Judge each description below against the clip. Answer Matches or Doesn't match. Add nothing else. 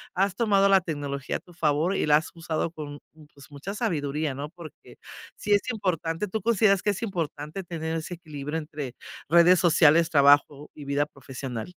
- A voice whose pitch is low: Doesn't match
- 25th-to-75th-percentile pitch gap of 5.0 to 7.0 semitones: Doesn't match